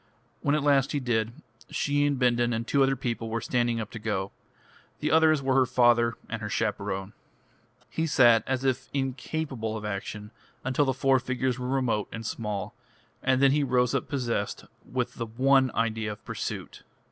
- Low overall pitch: Yes, low, 125 Hz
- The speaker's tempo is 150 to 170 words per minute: No, average, 180 wpm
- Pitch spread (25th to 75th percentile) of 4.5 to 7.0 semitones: No, average, 3.1 semitones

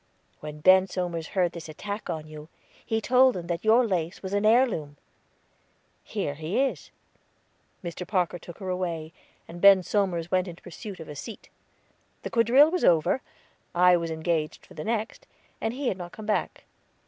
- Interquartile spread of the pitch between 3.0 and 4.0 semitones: No, average, 4.6 semitones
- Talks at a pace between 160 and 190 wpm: Yes, average, 175 wpm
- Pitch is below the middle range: No, medium, 180 Hz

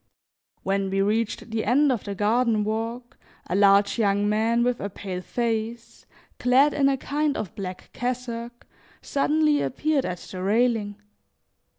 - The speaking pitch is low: No, high, 230 Hz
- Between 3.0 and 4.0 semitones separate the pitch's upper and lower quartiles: Yes, average, 3.6 semitones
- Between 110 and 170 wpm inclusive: Yes, average, 150 wpm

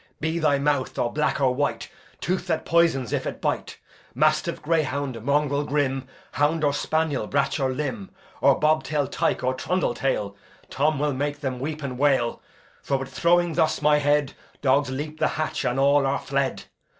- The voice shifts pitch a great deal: No, narrow, 2.4 semitones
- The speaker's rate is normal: Yes, average, 175 wpm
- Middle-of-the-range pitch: Yes, medium, 145 Hz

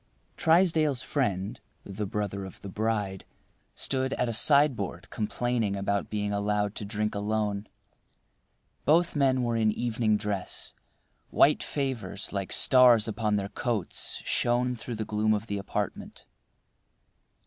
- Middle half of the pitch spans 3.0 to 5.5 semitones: Yes, average, 3.4 semitones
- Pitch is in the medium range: No, low, 110 Hz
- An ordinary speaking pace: No, slow, 130 wpm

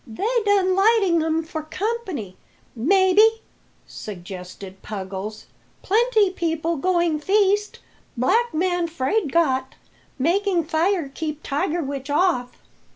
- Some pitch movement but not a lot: No, wide, 6.3 semitones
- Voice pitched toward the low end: No, very high, 335 Hz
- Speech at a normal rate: No, slow, 105 wpm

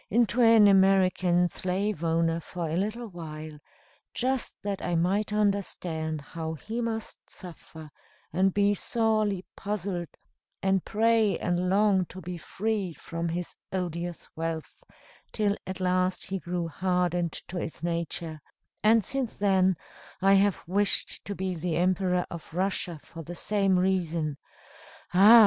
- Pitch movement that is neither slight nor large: Yes, average, 3.1 semitones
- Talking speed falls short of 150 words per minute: Yes, average, 140 wpm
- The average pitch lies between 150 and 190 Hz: Yes, medium, 185 Hz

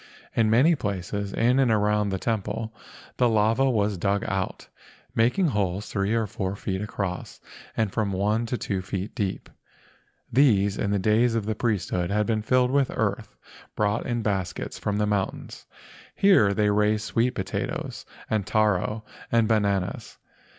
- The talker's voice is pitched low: Yes, low, 105 Hz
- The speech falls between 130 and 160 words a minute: Yes, average, 155 wpm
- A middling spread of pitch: No, narrow, 2.3 semitones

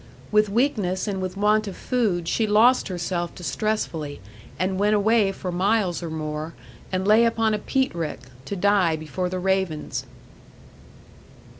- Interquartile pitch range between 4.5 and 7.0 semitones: No, average, 3.5 semitones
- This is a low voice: No, high, 190 Hz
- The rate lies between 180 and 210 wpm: No, average, 150 wpm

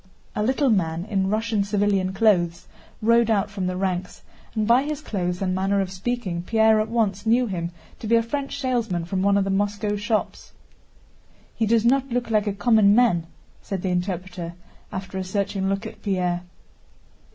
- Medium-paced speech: Yes, average, 185 wpm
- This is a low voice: No, high, 200 Hz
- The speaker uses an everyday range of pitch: Yes, average, 3.2 semitones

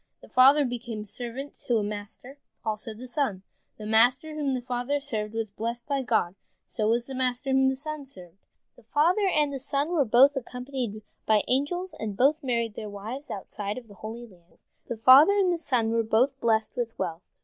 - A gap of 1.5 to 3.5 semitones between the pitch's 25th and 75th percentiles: No, average, 4.1 semitones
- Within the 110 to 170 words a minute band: No, fast, 205 wpm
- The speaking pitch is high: Yes, high, 245 Hz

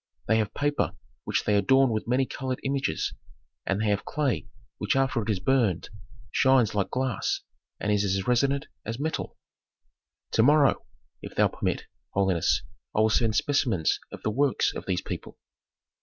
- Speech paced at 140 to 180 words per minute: Yes, average, 165 wpm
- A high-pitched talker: No, low, 115 Hz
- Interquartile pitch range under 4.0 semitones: No, average, 4.7 semitones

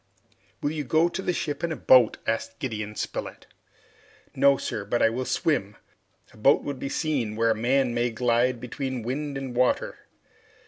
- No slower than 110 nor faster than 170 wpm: No, average, 180 wpm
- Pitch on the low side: Yes, low, 125 Hz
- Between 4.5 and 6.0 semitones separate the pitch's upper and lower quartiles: No, average, 3.7 semitones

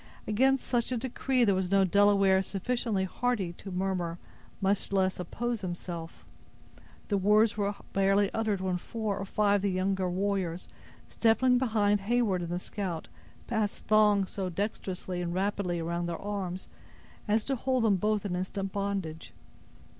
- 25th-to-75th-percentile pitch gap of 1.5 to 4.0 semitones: Yes, narrow, 2.5 semitones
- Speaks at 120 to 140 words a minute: No, average, 155 wpm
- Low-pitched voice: No, high, 200 Hz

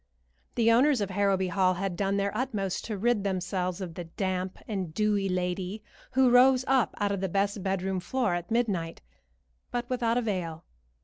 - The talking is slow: No, average, 175 wpm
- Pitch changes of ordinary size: Yes, average, 3.8 semitones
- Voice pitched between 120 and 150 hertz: No, high, 195 Hz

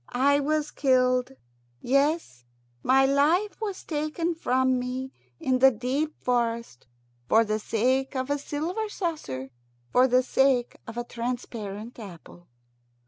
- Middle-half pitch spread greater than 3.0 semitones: Yes, average, 3.4 semitones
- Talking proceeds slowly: Yes, slow, 130 wpm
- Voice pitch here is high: Yes, very high, 260 Hz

